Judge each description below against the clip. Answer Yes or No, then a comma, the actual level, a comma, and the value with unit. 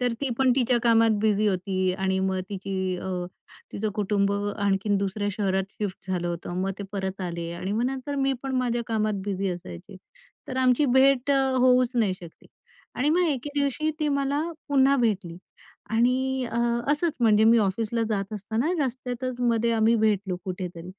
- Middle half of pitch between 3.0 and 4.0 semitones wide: No, average, 4.9 semitones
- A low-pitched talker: No, high, 220 Hz